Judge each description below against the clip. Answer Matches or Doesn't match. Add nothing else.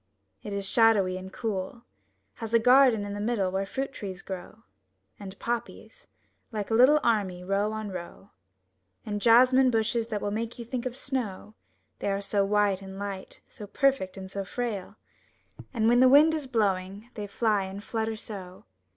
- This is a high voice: Matches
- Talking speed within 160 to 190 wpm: Matches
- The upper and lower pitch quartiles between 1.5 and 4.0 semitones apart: Matches